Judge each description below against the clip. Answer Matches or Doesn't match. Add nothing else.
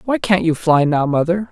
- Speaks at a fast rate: Matches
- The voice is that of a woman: Doesn't match